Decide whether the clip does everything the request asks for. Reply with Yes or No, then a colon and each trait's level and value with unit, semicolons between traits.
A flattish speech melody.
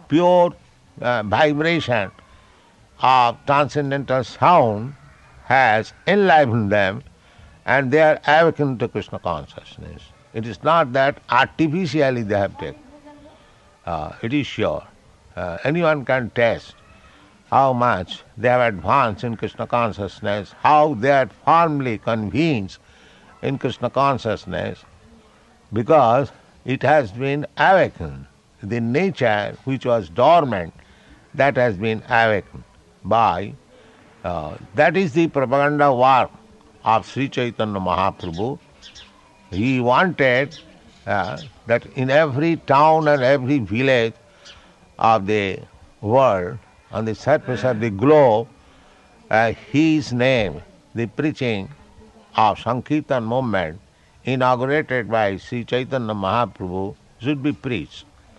No: average, 5.1 semitones